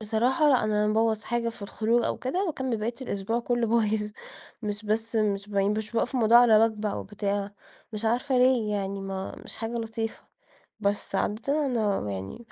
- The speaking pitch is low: No, high, 220 Hz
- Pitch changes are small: Yes, narrow, 2.3 semitones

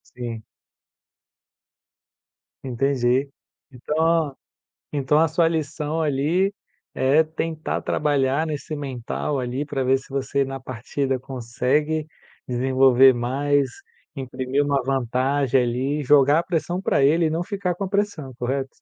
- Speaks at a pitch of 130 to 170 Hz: Yes, medium, 140 Hz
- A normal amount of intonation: Yes, average, 3.1 semitones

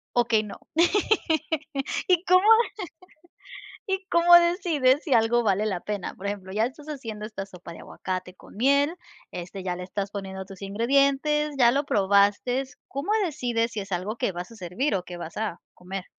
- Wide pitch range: Yes, wide, 6.9 semitones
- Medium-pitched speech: No, high, 225 Hz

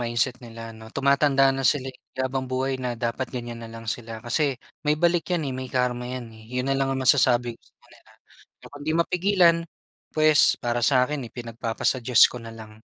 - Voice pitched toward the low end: Yes, low, 125 Hz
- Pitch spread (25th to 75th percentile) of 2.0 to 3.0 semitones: Yes, average, 2.7 semitones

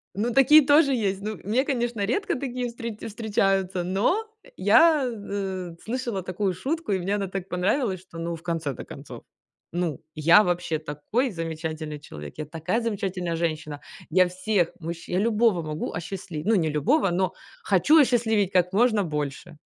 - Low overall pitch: No, high, 190 Hz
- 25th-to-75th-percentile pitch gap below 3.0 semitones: No, wide, 5.5 semitones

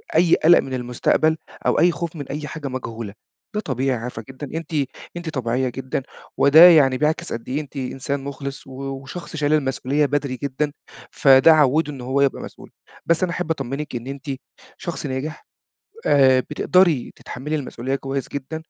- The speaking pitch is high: No, medium, 140 Hz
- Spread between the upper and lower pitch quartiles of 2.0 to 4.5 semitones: Yes, average, 2.9 semitones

